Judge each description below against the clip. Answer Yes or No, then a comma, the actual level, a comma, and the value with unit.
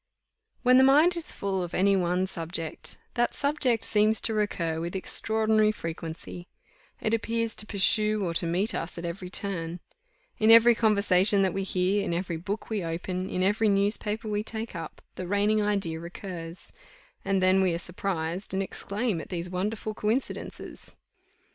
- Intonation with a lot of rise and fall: No, average, 3.4 semitones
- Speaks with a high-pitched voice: Yes, high, 195 Hz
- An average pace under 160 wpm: No, average, 165 wpm